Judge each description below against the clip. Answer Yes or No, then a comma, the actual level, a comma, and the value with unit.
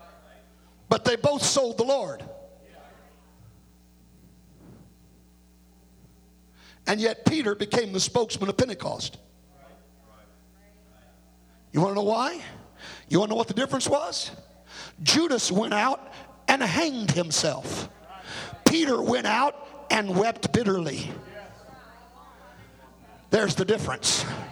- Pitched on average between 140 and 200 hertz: Yes, medium, 185 Hz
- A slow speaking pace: Yes, slow, 105 wpm